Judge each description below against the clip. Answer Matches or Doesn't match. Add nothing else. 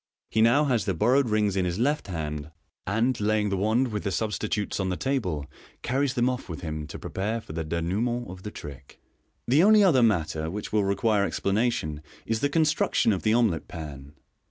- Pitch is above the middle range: Doesn't match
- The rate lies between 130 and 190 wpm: Doesn't match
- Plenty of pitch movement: Matches